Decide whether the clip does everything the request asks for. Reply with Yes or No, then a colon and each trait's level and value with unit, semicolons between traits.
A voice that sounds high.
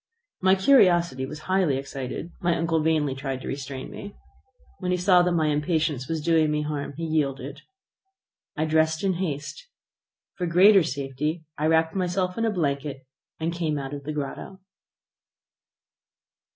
No: medium, 160 Hz